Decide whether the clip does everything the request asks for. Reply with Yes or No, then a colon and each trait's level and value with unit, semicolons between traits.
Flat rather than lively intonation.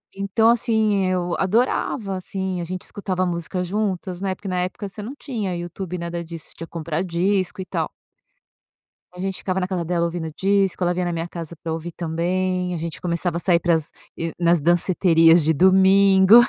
Yes: narrow, 2.1 semitones